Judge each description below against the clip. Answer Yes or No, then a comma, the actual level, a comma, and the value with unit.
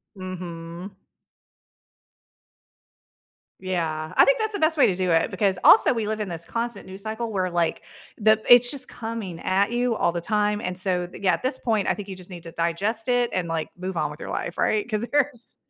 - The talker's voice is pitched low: No, high, 195 Hz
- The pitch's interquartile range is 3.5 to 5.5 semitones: Yes, average, 4.6 semitones